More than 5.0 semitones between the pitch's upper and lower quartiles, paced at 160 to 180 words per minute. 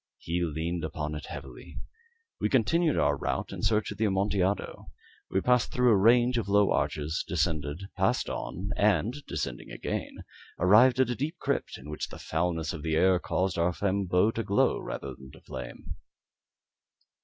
Yes: wide, 5.6 semitones; average, 165 wpm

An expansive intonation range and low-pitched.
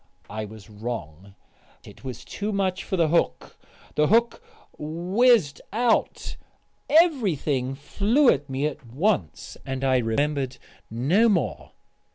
No: wide, 8.3 semitones; medium, 150 Hz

